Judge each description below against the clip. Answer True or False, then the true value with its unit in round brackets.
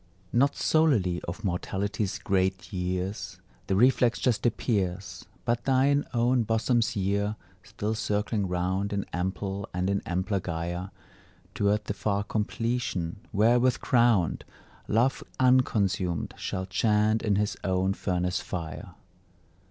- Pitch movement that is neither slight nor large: True (3.7 semitones)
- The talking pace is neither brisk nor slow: False (120 wpm)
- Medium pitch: False (100 Hz)